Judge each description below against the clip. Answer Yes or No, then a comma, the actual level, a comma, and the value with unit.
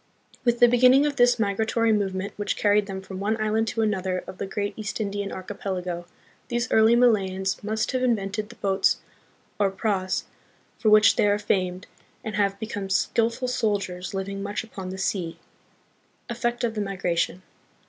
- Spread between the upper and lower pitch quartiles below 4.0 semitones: Yes, average, 2.7 semitones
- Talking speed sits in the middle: Yes, average, 170 wpm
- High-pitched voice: Yes, high, 205 Hz